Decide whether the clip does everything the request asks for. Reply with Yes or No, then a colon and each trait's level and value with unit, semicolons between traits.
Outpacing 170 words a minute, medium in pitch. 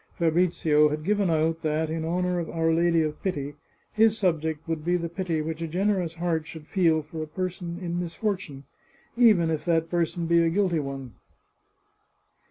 Yes: average, 180 wpm; medium, 165 Hz